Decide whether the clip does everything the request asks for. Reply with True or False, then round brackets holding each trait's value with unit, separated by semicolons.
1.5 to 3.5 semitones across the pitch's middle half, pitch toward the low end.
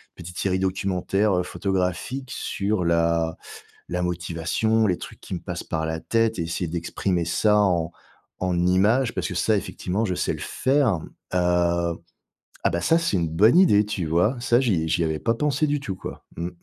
False (4.3 semitones; 90 Hz)